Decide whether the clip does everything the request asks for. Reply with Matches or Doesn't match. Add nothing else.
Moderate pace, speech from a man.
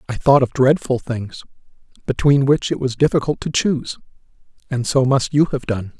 Matches